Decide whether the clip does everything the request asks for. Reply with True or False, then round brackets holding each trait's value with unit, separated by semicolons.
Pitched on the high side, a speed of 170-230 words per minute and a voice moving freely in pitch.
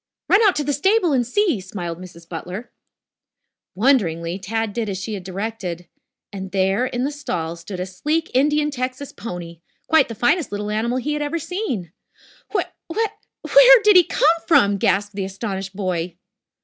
True (220 Hz; 175 wpm; 7.8 semitones)